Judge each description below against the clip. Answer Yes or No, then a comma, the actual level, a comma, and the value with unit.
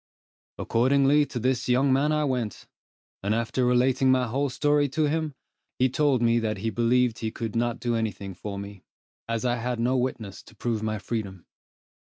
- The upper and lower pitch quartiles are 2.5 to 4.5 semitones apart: Yes, average, 2.9 semitones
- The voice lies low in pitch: Yes, low, 125 Hz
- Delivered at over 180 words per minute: Yes, average, 190 wpm